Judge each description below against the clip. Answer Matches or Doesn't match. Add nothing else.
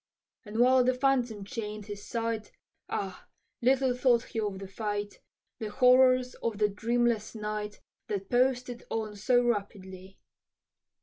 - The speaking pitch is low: Doesn't match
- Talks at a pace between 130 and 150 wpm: Matches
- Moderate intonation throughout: Matches